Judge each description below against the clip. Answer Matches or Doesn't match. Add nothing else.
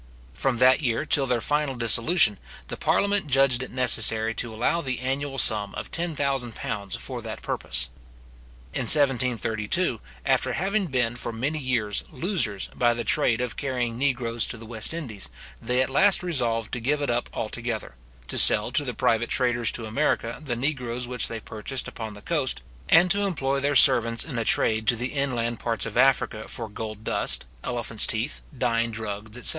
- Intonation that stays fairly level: Doesn't match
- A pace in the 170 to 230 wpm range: Matches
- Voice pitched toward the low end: Matches